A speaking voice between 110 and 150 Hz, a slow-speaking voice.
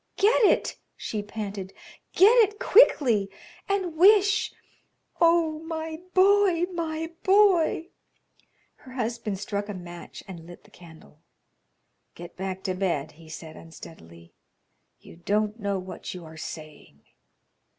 No: high, 210 Hz; slow, 125 wpm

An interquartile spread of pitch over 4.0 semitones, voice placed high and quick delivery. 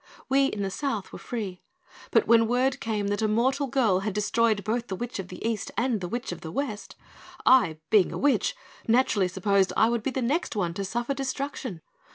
Yes: average, 4.5 semitones; high, 225 Hz; fast, 210 wpm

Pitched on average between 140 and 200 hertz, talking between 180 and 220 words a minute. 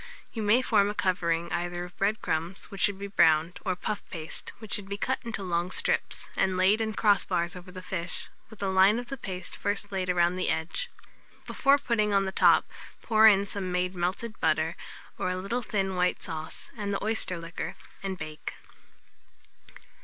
Yes: high, 190 Hz; average, 195 wpm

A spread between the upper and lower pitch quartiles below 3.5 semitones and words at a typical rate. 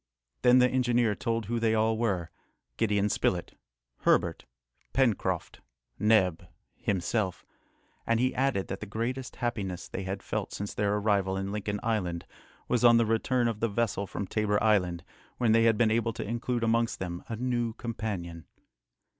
Yes: average, 3.0 semitones; average, 165 wpm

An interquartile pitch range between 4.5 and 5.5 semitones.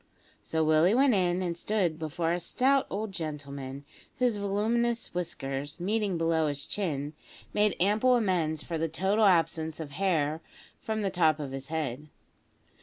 Yes: average, 4.9 semitones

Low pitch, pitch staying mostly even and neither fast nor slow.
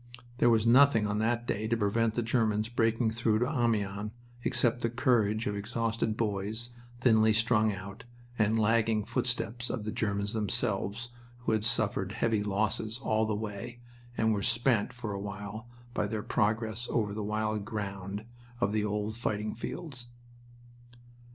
Yes: low, 110 Hz; narrow, 1.9 semitones; average, 160 wpm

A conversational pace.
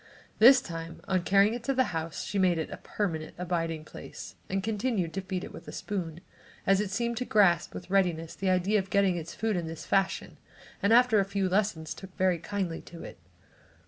No: fast, 210 wpm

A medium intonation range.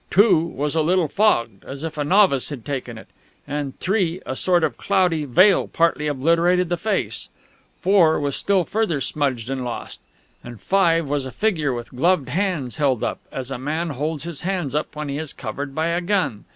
Yes: average, 4.8 semitones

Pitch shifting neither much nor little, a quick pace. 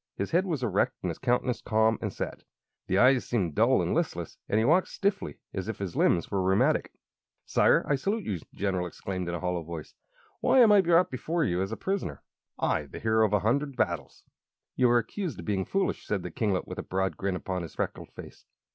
No: wide, 6.7 semitones; fast, 225 wpm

